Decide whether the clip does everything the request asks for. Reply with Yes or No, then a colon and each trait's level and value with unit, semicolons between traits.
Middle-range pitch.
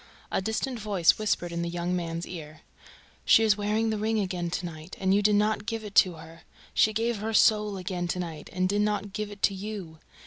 No: high, 200 Hz